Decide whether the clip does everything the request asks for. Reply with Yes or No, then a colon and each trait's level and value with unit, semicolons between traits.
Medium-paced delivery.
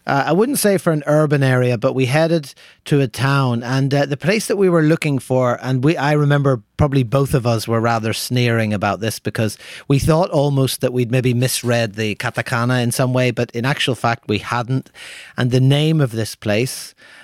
No: fast, 210 wpm